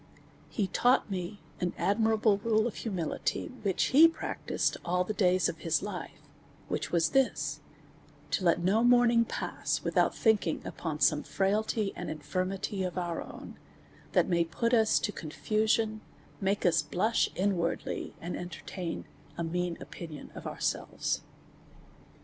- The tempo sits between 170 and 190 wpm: No, average, 140 wpm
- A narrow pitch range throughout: No, average, 4.0 semitones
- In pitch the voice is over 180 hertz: Yes, high, 190 Hz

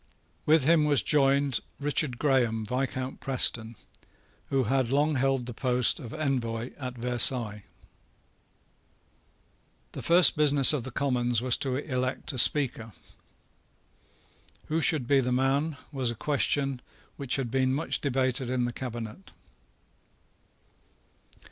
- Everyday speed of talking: No, slow, 125 wpm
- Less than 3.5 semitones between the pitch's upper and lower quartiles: Yes, narrow, 2.5 semitones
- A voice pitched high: No, low, 130 Hz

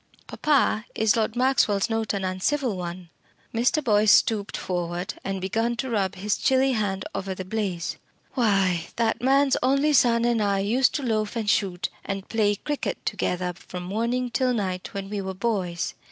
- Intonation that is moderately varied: Yes, average, 3.9 semitones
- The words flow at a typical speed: Yes, average, 170 wpm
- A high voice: Yes, high, 210 Hz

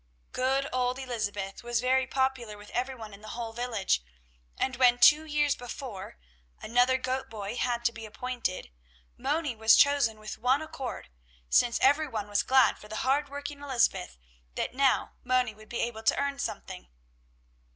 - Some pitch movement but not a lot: Yes, average, 3.2 semitones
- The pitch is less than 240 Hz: No, high, 245 Hz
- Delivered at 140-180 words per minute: Yes, average, 170 wpm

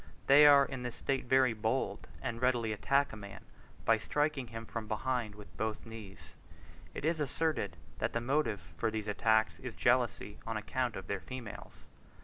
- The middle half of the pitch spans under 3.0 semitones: No, average, 3.9 semitones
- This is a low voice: Yes, low, 115 Hz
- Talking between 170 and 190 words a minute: Yes, average, 175 wpm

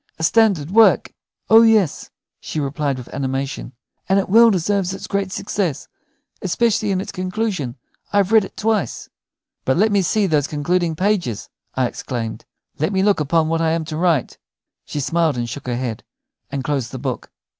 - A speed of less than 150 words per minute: No, average, 180 wpm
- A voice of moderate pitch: Yes, medium, 165 Hz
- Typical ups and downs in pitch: No, wide, 6.4 semitones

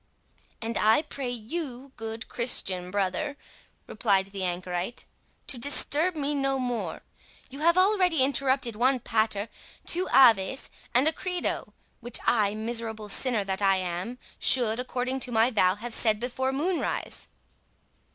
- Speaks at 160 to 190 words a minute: No, average, 140 wpm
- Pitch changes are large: No, average, 4.3 semitones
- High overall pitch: Yes, high, 240 Hz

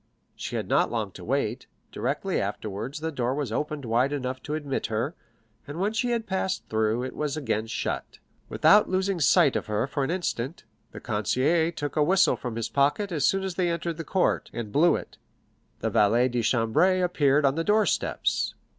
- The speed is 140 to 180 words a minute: No, average, 200 wpm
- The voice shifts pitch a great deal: Yes, wide, 6.1 semitones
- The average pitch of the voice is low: No, medium, 145 Hz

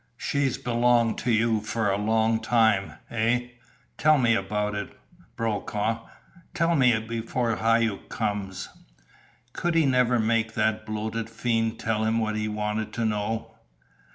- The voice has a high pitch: No, low, 115 Hz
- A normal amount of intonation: No, narrow, 1.5 semitones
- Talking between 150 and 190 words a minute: No, average, 140 wpm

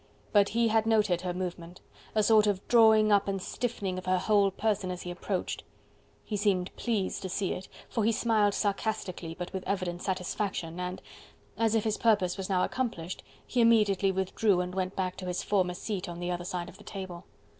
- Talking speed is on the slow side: No, average, 200 wpm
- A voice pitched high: Yes, high, 195 Hz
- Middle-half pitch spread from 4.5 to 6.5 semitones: No, average, 2.9 semitones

